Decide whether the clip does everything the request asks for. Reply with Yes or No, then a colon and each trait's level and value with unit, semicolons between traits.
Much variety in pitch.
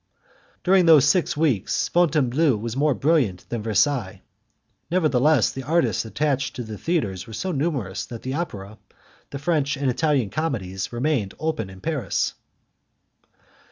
Yes: wide, 6.1 semitones